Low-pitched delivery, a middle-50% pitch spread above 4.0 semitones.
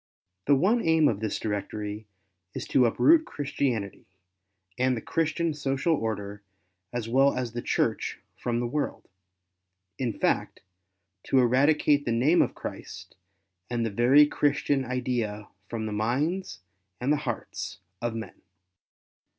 Yes: low, 120 Hz; average, 4.8 semitones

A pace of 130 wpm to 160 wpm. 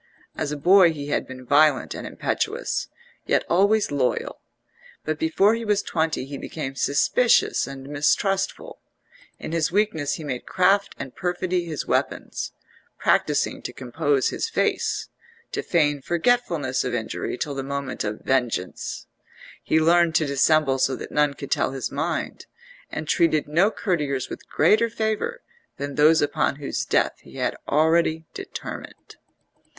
Yes: average, 150 wpm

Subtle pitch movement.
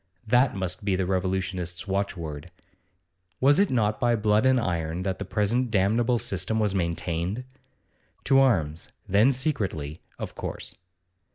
No: average, 4.7 semitones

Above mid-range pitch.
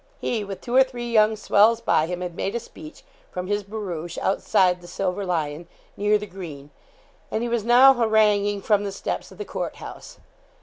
Yes: high, 205 Hz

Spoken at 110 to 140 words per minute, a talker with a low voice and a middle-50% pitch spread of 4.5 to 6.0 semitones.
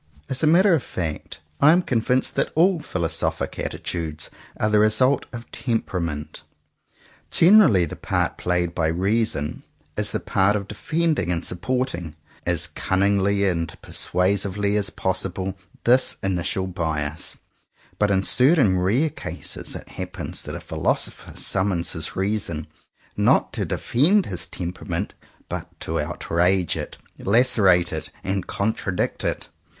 Yes: slow, 135 wpm; very low, 95 Hz; average, 5.2 semitones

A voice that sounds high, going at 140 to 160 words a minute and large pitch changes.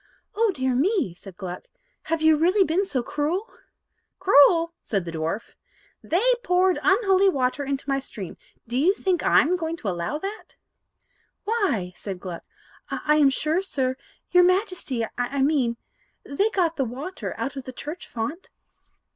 Yes: very high, 295 Hz; average, 155 wpm; wide, 6.7 semitones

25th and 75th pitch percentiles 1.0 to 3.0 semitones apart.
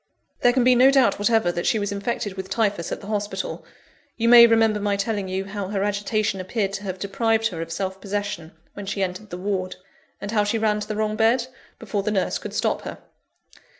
Yes: narrow, 2.4 semitones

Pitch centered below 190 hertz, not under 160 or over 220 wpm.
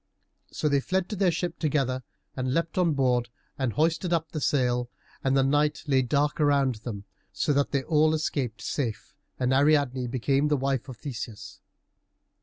Yes: medium, 140 Hz; average, 175 wpm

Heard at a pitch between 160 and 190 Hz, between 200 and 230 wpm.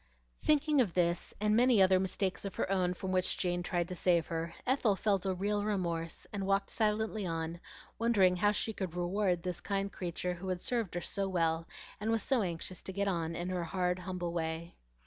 Yes: medium, 185 Hz; fast, 205 wpm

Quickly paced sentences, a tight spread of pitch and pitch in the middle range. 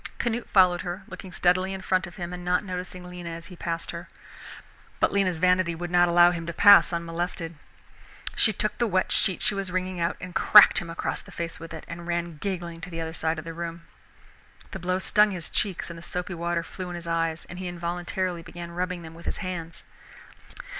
Yes: fast, 220 wpm; narrow, 1.5 semitones; medium, 175 Hz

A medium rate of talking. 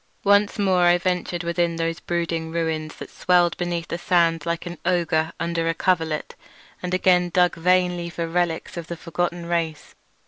Yes: average, 170 wpm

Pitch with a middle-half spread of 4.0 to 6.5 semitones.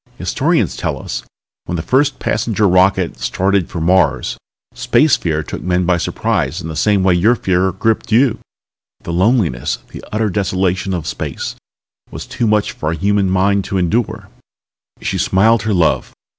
No: average, 3.4 semitones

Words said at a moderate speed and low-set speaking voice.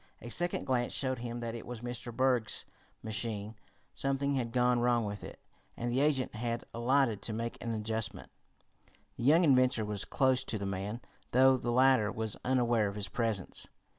Yes: average, 180 wpm; low, 120 Hz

